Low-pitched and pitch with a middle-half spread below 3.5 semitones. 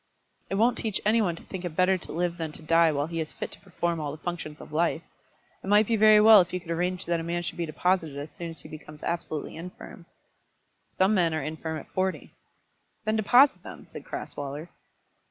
No: medium, 170 Hz; average, 3.1 semitones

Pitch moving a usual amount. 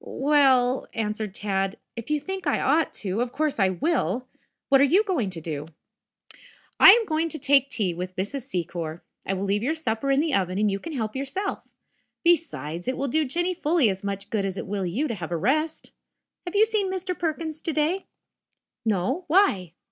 No: wide, 8.3 semitones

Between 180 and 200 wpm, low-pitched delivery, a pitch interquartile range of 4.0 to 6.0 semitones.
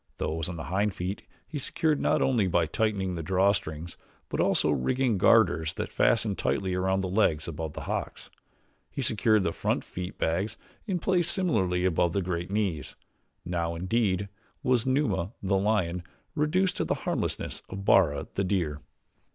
No: average, 165 wpm; very low, 95 Hz; average, 4.4 semitones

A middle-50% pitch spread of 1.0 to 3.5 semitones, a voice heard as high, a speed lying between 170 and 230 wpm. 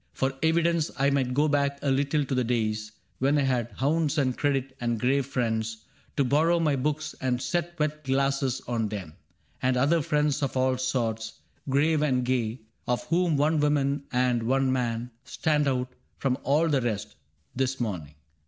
No: average, 3.1 semitones; low, 135 Hz; average, 175 wpm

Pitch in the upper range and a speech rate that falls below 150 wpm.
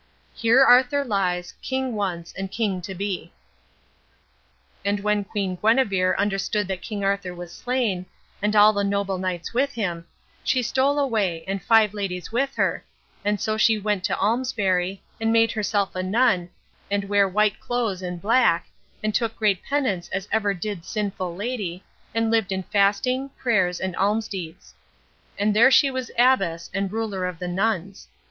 No: high, 205 Hz; average, 165 wpm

